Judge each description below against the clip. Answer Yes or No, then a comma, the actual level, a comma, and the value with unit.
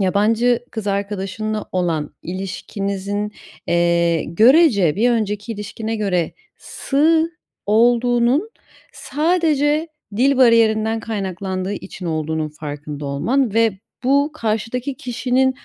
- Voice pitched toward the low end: No, high, 215 Hz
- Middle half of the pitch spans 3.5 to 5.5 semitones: Yes, average, 4.7 semitones